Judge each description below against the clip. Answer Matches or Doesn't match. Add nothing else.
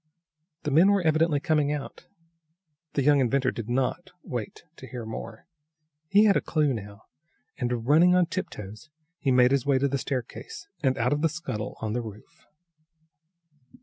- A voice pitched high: Doesn't match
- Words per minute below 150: Doesn't match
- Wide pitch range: Doesn't match